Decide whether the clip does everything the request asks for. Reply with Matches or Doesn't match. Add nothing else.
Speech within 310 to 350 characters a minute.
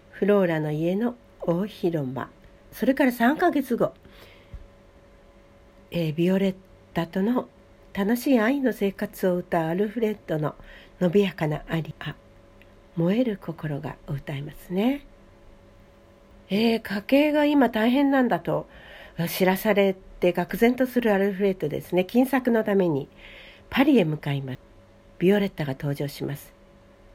Doesn't match